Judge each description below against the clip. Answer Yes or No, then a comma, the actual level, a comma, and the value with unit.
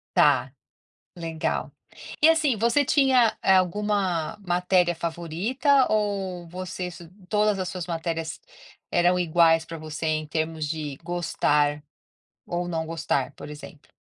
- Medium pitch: Yes, medium, 175 Hz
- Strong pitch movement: No, average, 3.5 semitones